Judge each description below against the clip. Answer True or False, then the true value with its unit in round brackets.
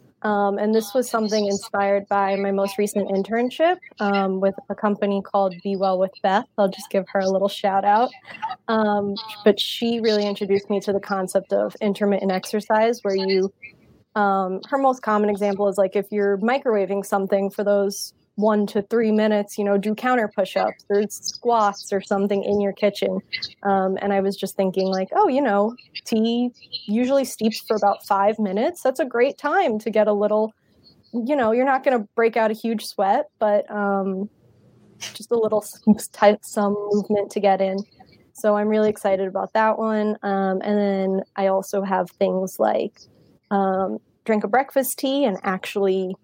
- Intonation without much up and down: True (1.9 semitones)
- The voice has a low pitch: False (205 Hz)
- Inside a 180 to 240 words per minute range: True (185 wpm)